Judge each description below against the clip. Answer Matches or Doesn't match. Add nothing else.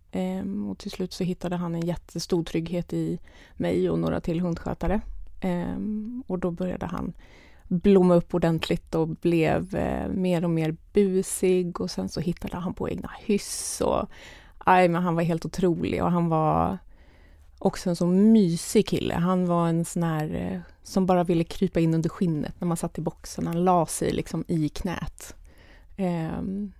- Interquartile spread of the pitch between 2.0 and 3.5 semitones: Matches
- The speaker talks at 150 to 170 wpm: Matches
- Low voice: Doesn't match